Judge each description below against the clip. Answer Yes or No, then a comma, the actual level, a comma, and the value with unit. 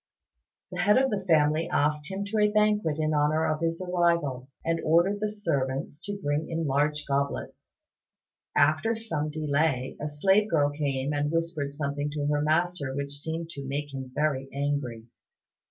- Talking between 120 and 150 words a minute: No, average, 170 wpm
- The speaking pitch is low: No, medium, 150 Hz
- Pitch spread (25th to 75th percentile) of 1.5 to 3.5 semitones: Yes, average, 2.9 semitones